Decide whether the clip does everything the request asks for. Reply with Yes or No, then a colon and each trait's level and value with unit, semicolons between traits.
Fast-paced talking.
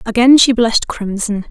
No: average, 160 wpm